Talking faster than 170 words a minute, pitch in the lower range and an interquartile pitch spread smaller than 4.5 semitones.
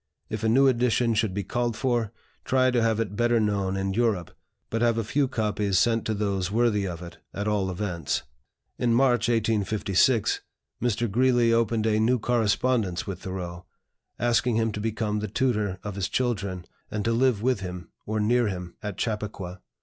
Yes: average, 180 wpm; low, 110 Hz; average, 3.1 semitones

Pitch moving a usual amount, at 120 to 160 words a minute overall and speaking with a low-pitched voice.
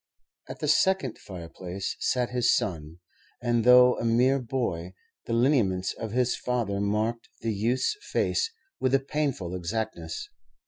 Yes: average, 4.5 semitones; average, 140 wpm; low, 115 Hz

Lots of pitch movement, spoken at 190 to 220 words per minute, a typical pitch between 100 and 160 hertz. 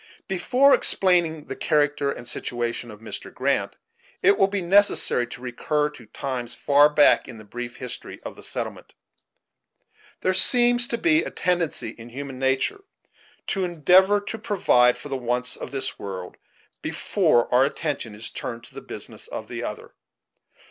No: wide, 7.3 semitones; average, 160 wpm; medium, 140 Hz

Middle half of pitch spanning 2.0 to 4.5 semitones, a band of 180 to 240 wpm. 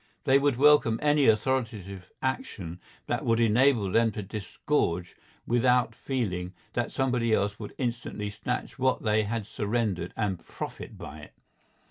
No: average, 3.7 semitones; average, 140 wpm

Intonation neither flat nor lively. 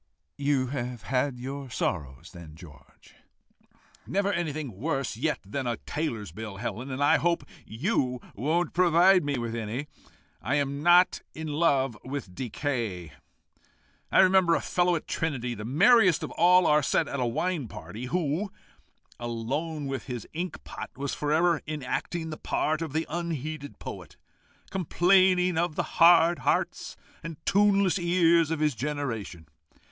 No: wide, 5.7 semitones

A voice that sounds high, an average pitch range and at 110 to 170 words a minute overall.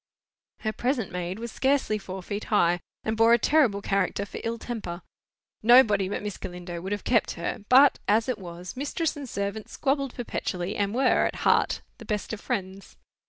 No: high, 210 Hz; average, 4.1 semitones; average, 185 wpm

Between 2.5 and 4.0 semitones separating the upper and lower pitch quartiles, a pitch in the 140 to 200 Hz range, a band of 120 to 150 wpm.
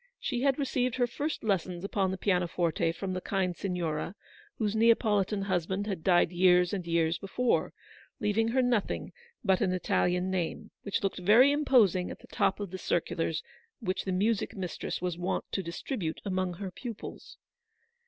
No: average, 3.4 semitones; high, 190 Hz; average, 170 wpm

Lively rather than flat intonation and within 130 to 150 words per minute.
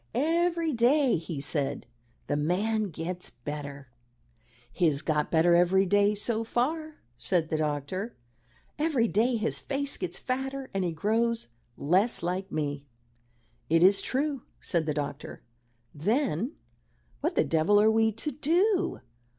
Yes: wide, 7.9 semitones; average, 140 wpm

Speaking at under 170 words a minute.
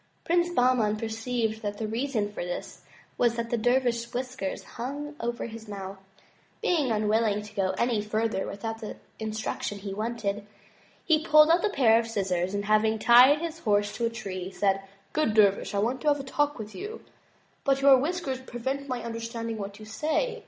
No: average, 190 wpm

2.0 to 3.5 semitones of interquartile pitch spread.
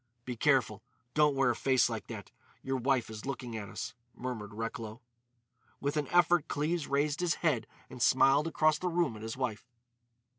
No: average, 4.7 semitones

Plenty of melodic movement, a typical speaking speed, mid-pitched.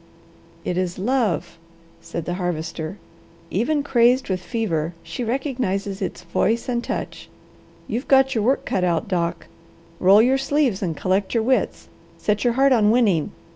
No: wide, 5.8 semitones; average, 155 wpm; high, 210 Hz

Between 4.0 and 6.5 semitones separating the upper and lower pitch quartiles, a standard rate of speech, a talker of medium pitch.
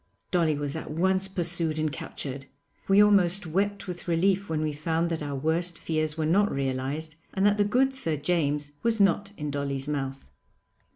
Yes: average, 4.5 semitones; average, 180 wpm; medium, 160 Hz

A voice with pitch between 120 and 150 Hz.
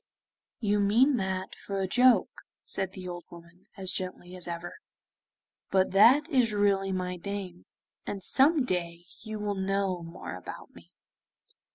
No: high, 190 Hz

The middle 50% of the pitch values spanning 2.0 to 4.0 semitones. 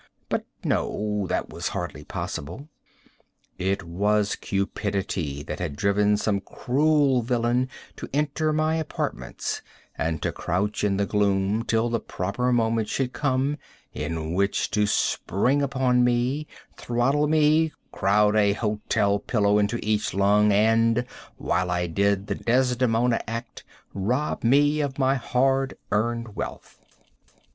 No: average, 4.4 semitones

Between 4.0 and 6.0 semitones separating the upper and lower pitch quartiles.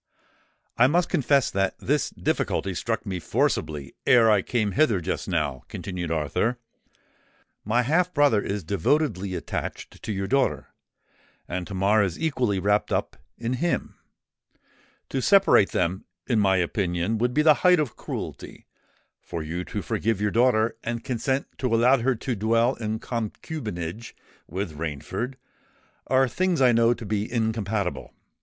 Yes: average, 5.0 semitones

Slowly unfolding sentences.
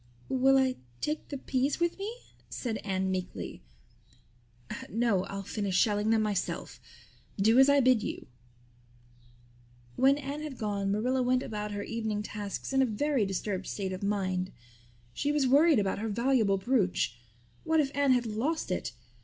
No: average, 160 wpm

